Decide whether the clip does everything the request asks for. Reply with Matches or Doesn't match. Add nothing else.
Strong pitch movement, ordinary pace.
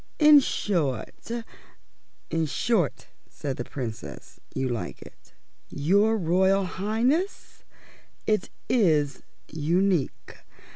Doesn't match